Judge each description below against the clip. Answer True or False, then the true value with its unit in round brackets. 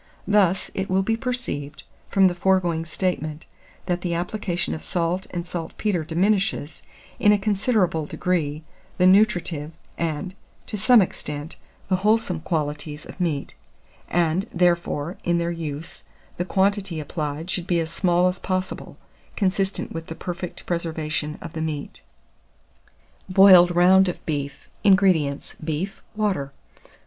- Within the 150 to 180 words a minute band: False (135 wpm)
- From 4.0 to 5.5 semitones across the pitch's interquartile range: False (3.1 semitones)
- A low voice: False (175 Hz)